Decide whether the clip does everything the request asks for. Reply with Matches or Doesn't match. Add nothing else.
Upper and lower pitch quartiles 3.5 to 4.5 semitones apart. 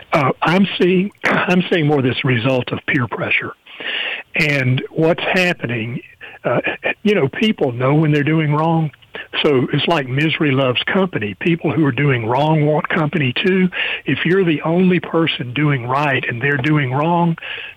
Matches